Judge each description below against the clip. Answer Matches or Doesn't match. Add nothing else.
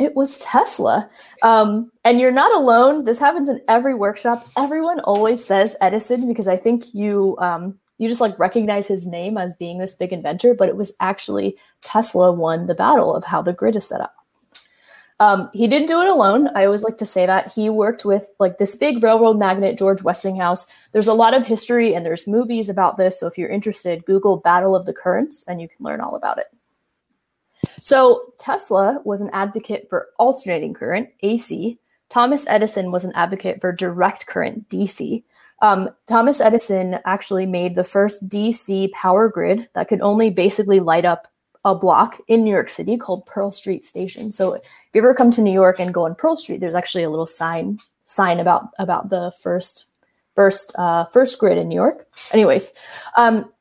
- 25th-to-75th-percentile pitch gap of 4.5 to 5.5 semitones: Doesn't match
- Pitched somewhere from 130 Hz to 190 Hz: Doesn't match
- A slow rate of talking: Doesn't match